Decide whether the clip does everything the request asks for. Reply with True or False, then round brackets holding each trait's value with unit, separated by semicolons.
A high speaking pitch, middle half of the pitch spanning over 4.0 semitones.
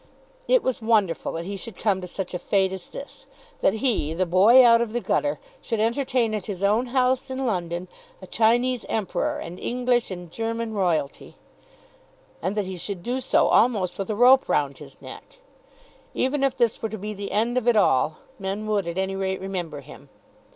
True (215 Hz; 4.5 semitones)